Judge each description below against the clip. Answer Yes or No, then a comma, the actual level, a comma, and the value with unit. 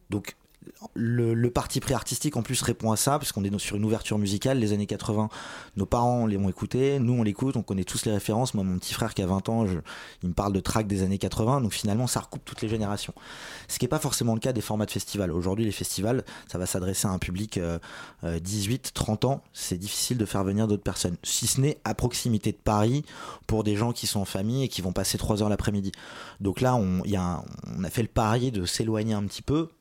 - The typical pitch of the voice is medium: No, low, 110 Hz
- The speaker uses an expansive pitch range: No, average, 3.6 semitones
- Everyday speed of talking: No, fast, 250 wpm